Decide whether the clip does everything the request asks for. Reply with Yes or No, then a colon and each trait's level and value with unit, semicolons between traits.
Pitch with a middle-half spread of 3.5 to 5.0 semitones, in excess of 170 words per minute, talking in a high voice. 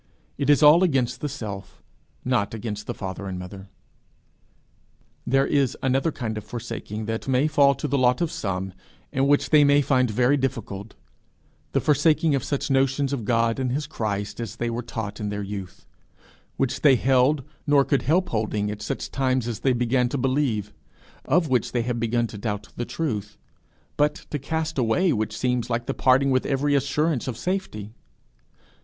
No: average, 4.4 semitones; average, 180 wpm; low, 125 Hz